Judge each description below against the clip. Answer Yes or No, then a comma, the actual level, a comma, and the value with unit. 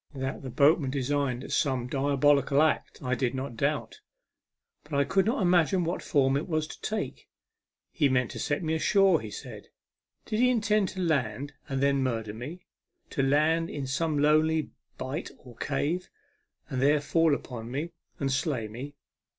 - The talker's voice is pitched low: No, medium, 145 Hz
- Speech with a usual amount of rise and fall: Yes, average, 3.4 semitones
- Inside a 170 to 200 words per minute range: Yes, average, 175 wpm